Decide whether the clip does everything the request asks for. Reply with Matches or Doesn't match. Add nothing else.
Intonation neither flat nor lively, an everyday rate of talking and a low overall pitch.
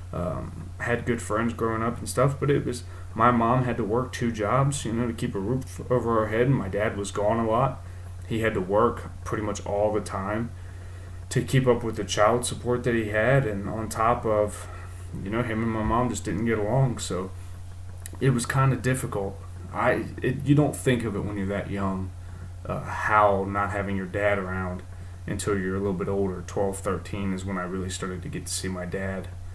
Doesn't match